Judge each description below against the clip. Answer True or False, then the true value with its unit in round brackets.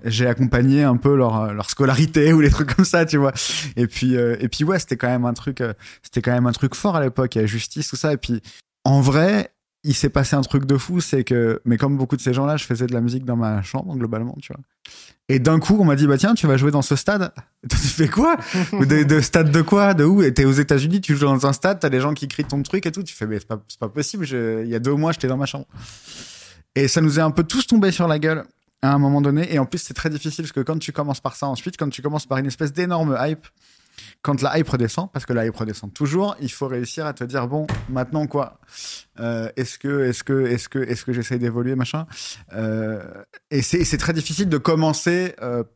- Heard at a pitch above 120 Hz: True (140 Hz)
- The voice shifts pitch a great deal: False (4.1 semitones)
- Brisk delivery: True (270 wpm)